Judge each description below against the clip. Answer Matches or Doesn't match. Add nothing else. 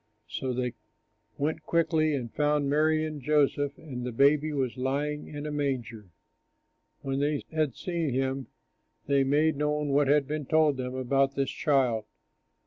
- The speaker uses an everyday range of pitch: Doesn't match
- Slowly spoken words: Doesn't match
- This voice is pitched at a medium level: Matches